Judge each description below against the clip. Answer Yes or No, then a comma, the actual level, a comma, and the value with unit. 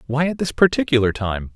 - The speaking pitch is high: No, medium, 140 Hz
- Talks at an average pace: Yes, average, 195 wpm